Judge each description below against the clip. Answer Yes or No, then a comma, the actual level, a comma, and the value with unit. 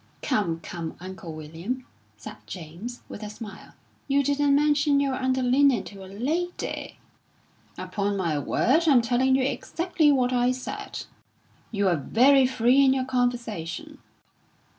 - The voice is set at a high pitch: Yes, very high, 250 Hz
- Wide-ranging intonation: Yes, wide, 5.8 semitones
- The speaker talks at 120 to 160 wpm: Yes, average, 140 wpm